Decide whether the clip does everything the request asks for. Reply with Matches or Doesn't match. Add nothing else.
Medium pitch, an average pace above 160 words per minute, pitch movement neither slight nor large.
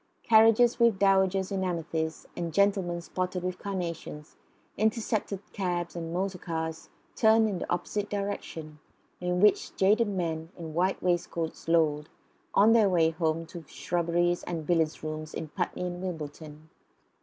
Doesn't match